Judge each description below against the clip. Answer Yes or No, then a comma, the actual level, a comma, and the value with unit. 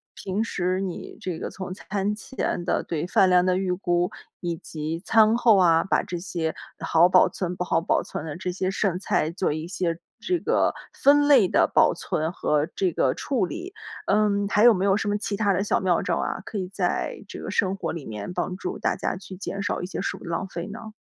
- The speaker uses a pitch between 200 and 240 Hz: No, medium, 185 Hz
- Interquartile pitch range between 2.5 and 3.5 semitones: Yes, average, 2.9 semitones